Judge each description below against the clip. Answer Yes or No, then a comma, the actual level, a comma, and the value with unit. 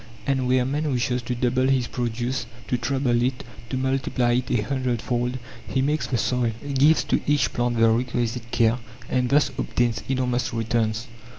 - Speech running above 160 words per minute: Yes, average, 175 wpm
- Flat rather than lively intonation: Yes, narrow, 1.7 semitones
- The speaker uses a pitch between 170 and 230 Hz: No, low, 125 Hz